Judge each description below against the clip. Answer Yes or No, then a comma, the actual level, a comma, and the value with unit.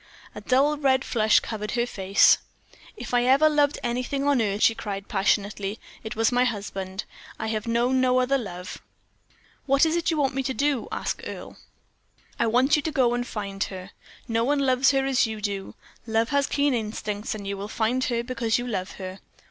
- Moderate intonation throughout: Yes, average, 4.2 semitones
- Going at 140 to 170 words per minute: No, average, 195 wpm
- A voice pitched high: Yes, high, 235 Hz